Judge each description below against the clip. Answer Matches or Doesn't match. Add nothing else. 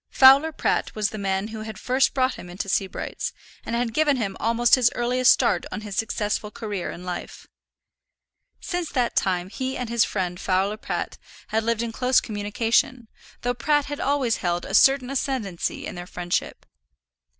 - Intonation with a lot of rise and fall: Doesn't match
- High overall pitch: Matches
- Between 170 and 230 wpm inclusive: Matches